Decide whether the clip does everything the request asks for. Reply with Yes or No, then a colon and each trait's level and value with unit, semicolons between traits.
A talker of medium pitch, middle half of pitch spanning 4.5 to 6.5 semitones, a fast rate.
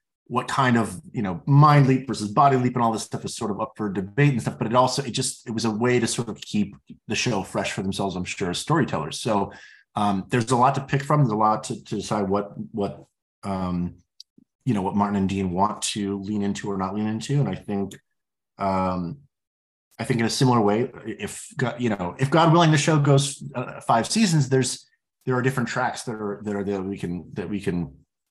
No: low, 115 Hz; average, 4.8 semitones; fast, 240 wpm